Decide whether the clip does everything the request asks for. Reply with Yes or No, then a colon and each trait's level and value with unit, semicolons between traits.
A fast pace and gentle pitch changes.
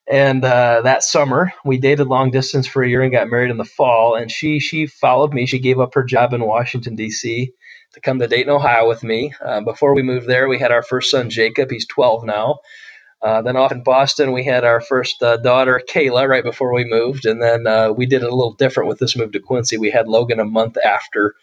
Yes: fast, 245 wpm; narrow, 2.3 semitones